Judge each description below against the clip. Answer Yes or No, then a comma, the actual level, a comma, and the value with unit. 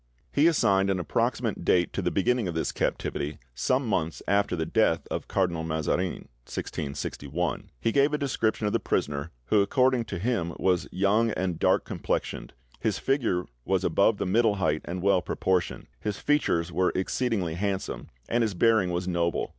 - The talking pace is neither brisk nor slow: Yes, average, 170 wpm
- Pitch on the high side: No, very low, 95 Hz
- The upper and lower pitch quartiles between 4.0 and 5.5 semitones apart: Yes, average, 4.6 semitones